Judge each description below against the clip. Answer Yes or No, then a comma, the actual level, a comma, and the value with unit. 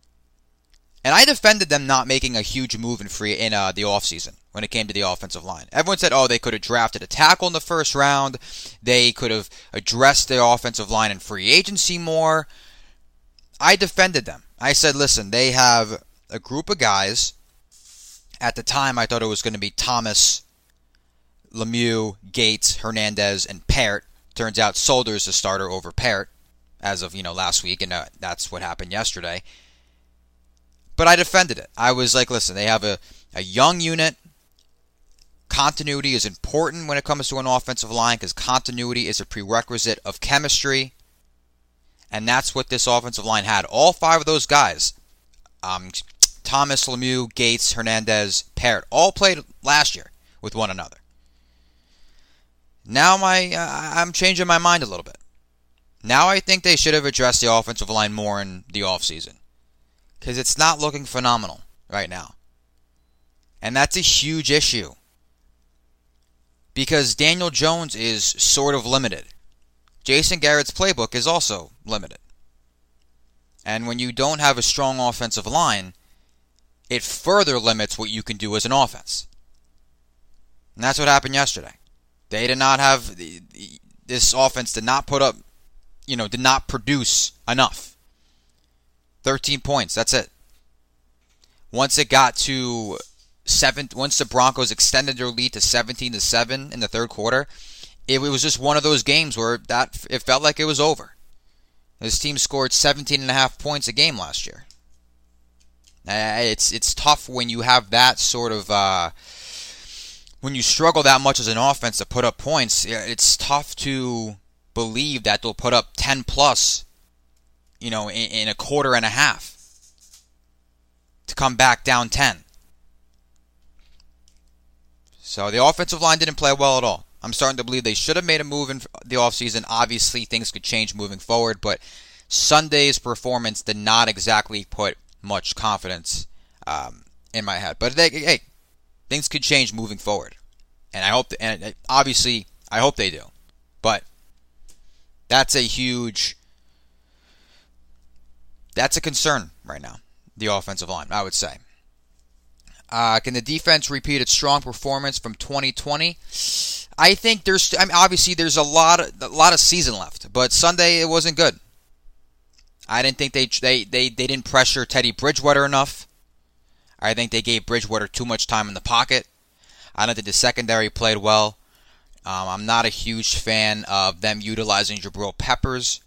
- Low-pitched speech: Yes, low, 110 Hz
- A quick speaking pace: No, average, 165 wpm